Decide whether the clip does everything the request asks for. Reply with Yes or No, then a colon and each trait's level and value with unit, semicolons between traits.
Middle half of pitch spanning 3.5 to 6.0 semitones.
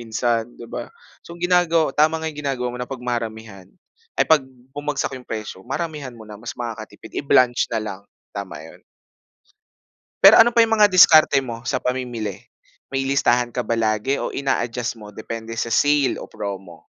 Yes: average, 4.7 semitones